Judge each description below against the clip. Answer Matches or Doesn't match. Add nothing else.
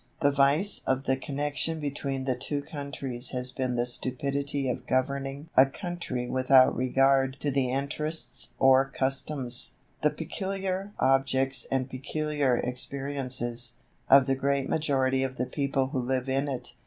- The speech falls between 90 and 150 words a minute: Matches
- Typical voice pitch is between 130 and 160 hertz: Matches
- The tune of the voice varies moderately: Doesn't match